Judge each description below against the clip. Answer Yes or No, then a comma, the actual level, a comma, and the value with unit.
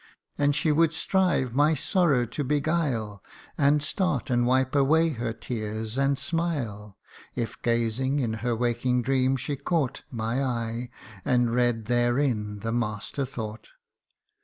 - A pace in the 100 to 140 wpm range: Yes, slow, 135 wpm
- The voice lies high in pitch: No, low, 125 Hz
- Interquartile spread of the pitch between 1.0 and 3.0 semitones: No, average, 3.8 semitones